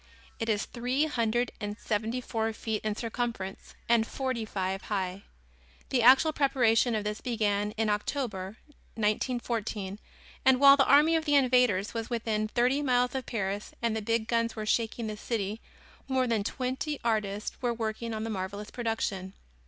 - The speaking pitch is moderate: No, high, 225 Hz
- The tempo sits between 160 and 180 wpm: Yes, average, 165 wpm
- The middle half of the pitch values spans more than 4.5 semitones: No, average, 3.0 semitones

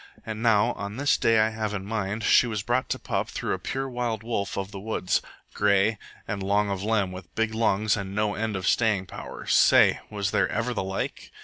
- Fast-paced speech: Yes, fast, 220 wpm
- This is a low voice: Yes, low, 105 Hz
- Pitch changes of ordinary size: No, narrow, 2.2 semitones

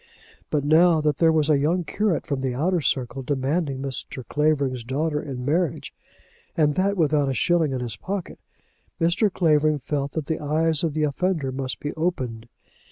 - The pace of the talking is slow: No, average, 175 wpm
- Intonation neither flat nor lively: Yes, average, 3.3 semitones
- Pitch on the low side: No, medium, 150 Hz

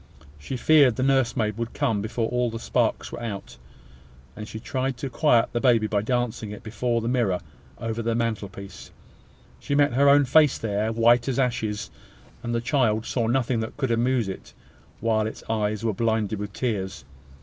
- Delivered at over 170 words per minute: Yes, average, 180 wpm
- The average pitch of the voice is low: Yes, low, 115 Hz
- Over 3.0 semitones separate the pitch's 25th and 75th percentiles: No, narrow, 2.5 semitones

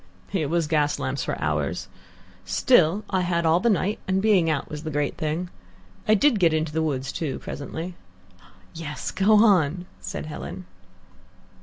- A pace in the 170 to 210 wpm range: No, average, 160 wpm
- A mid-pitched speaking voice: Yes, medium, 165 Hz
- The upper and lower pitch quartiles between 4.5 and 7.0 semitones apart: No, average, 3.8 semitones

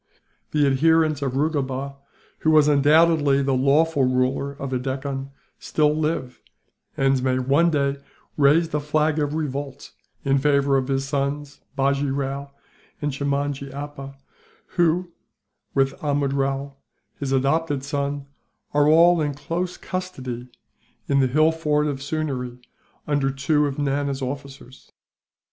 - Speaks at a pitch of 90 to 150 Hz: Yes, medium, 140 Hz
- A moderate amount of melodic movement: No, narrow, 1.8 semitones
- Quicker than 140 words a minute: No, slow, 135 wpm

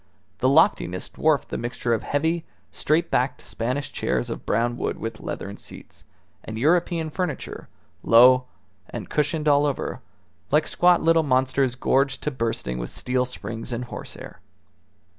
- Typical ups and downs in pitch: Yes, average, 4.4 semitones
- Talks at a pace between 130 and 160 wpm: Yes, average, 145 wpm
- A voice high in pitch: No, low, 130 Hz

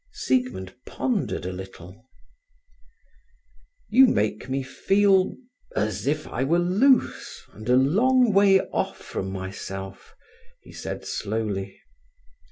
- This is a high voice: No, low, 130 Hz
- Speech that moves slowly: Yes, slow, 105 wpm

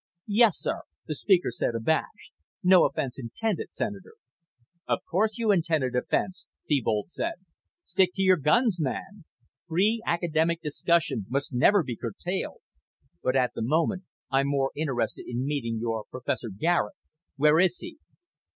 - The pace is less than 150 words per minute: Yes, average, 140 wpm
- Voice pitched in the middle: Yes, medium, 160 Hz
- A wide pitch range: Yes, wide, 6.7 semitones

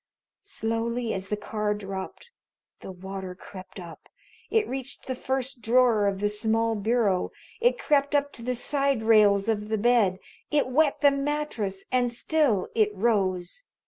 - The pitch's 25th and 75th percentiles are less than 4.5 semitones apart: No, average, 4.9 semitones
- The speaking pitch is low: No, high, 225 Hz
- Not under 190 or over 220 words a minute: No, average, 155 wpm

